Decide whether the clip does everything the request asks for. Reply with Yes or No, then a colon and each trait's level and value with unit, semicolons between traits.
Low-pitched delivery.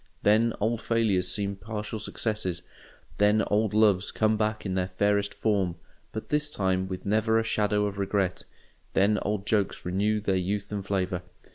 Yes: low, 105 Hz